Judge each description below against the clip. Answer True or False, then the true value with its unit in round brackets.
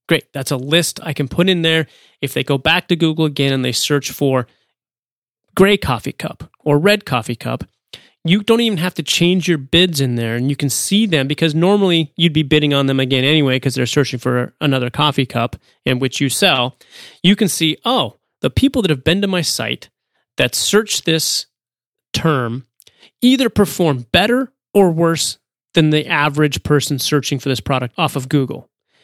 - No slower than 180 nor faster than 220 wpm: True (195 wpm)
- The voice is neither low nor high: True (150 Hz)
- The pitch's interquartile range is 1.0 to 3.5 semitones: False (4.6 semitones)